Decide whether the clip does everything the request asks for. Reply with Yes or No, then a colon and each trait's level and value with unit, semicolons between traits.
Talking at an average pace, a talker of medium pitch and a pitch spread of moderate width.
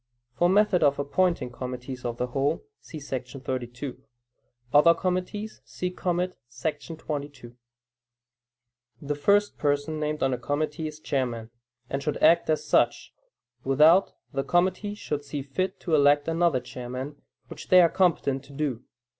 Yes: average, 145 wpm; medium, 145 Hz; average, 4.4 semitones